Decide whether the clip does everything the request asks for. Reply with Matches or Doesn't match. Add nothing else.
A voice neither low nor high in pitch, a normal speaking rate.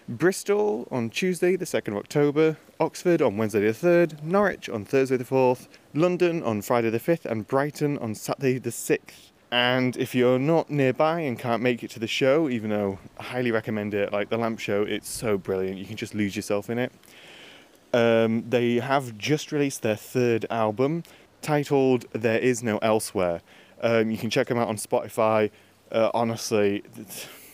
Doesn't match